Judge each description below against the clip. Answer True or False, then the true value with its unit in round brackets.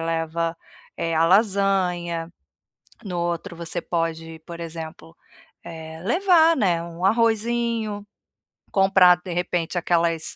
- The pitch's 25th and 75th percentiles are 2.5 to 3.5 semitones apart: True (3.2 semitones)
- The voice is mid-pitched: True (175 Hz)